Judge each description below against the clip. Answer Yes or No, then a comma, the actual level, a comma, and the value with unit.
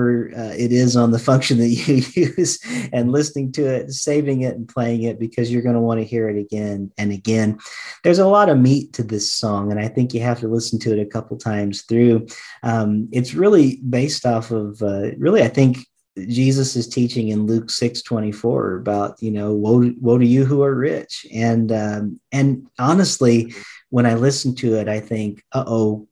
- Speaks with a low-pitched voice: Yes, low, 120 Hz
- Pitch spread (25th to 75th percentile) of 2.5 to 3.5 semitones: Yes, average, 2.9 semitones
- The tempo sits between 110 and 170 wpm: No, fast, 205 wpm